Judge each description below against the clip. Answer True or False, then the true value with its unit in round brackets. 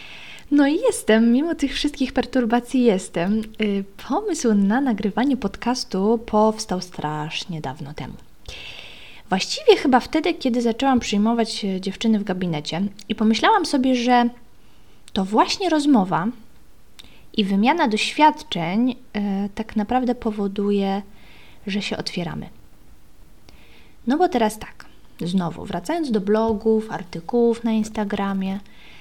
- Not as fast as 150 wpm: True (110 wpm)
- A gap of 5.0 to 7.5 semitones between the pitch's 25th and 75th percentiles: False (4.1 semitones)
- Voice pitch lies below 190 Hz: False (220 Hz)